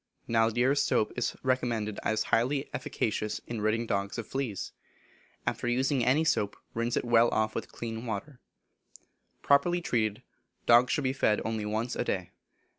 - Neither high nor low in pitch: No, low, 115 Hz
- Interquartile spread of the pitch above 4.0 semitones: No, average, 2.9 semitones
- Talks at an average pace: Yes, average, 155 wpm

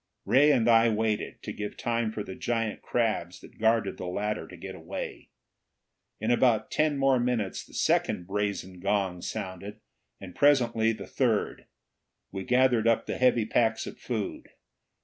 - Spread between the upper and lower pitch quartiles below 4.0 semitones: Yes, average, 2.9 semitones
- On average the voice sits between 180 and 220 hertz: No, low, 110 Hz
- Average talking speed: Yes, average, 160 wpm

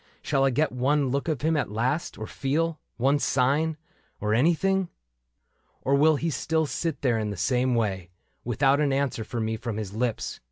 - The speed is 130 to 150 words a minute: No, average, 195 wpm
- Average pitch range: Yes, average, 4.7 semitones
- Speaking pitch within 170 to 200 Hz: No, low, 135 Hz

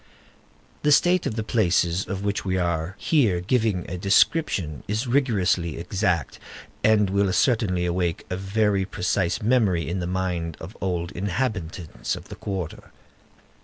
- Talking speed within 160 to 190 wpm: No, average, 145 wpm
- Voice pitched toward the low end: Yes, very low, 95 Hz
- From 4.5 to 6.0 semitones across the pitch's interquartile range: No, average, 3.5 semitones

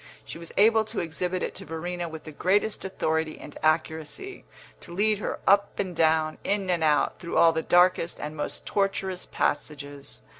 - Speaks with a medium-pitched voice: Yes, medium, 170 Hz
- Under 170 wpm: No, average, 180 wpm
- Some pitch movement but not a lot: Yes, average, 3.6 semitones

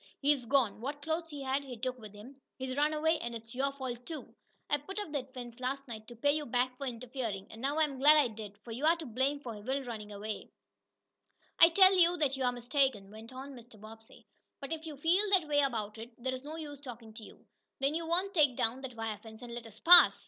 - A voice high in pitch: Yes, very high, 260 Hz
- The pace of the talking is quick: Yes, fast, 245 wpm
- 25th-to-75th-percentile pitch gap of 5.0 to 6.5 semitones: No, average, 4.0 semitones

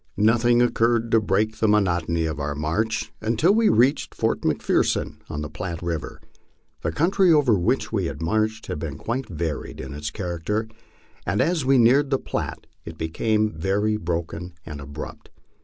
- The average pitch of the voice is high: No, low, 105 Hz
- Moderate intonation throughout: No, wide, 6.1 semitones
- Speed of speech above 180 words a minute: No, average, 170 wpm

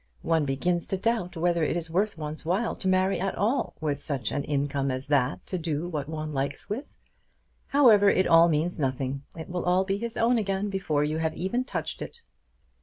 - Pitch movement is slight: No, average, 4.7 semitones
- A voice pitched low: No, medium, 170 Hz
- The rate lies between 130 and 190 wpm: No, fast, 205 wpm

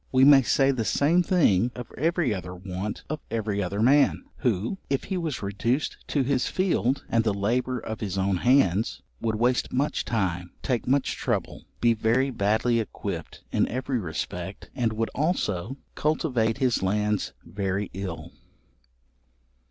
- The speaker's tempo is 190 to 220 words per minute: No, average, 155 wpm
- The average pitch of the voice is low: Yes, low, 115 Hz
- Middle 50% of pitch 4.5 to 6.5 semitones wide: Yes, average, 5.0 semitones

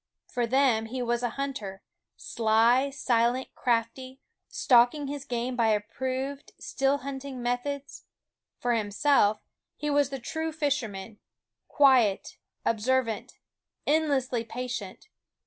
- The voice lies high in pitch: Yes, very high, 250 Hz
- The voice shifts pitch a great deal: No, average, 3.2 semitones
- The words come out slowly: Yes, slow, 110 wpm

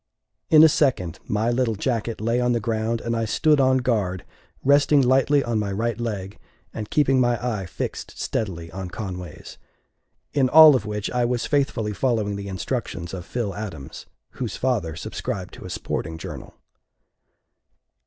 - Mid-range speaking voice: No, low, 115 Hz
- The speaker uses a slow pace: No, average, 165 wpm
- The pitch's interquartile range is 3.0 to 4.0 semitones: No, average, 4.4 semitones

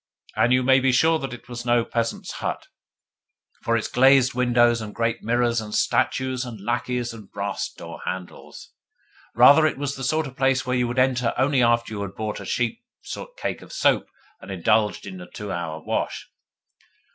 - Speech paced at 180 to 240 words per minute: Yes, average, 190 wpm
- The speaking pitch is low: Yes, low, 120 Hz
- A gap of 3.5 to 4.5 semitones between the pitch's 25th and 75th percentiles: No, average, 2.8 semitones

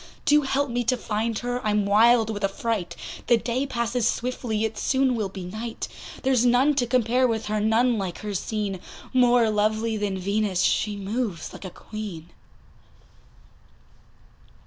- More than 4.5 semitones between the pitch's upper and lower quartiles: No, average, 2.8 semitones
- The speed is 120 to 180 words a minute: Yes, average, 155 wpm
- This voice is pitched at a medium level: No, high, 225 Hz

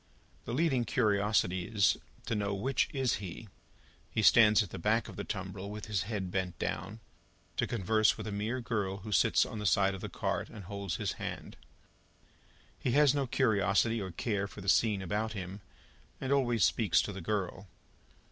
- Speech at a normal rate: Yes, average, 185 wpm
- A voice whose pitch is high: No, low, 105 Hz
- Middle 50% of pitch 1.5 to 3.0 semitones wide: Yes, average, 2.7 semitones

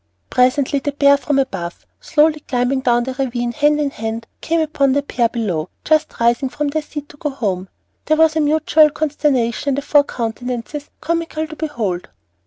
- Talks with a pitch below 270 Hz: No, very high, 280 Hz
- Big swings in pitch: No, average, 4.0 semitones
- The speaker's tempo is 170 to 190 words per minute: Yes, average, 185 wpm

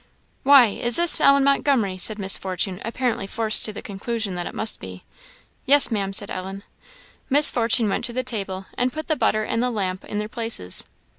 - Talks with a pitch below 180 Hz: No, high, 220 Hz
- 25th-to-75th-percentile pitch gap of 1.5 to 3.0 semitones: No, average, 4.3 semitones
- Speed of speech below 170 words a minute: No, average, 200 wpm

